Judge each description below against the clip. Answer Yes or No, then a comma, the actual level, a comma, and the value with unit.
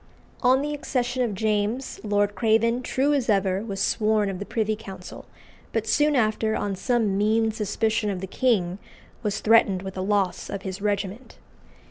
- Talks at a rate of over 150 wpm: Yes, average, 170 wpm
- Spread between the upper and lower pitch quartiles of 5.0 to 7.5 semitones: No, average, 2.7 semitones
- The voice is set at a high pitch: Yes, high, 215 Hz